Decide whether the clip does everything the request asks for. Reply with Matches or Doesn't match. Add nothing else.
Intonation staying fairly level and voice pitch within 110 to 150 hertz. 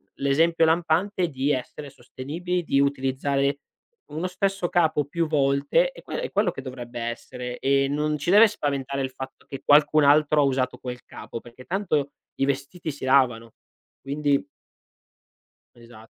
Doesn't match